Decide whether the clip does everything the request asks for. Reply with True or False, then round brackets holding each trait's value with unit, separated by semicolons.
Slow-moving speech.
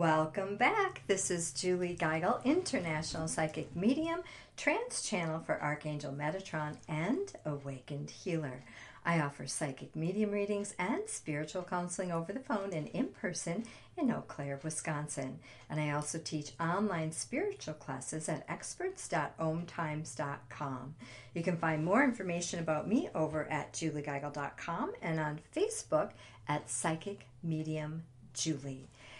True (125 wpm)